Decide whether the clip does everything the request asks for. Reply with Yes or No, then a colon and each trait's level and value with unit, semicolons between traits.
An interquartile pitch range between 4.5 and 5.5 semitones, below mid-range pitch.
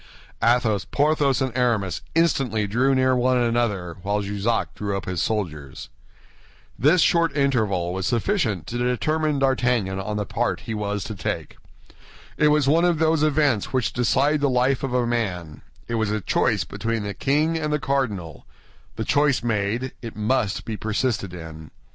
Yes: average, 5.1 semitones; low, 120 Hz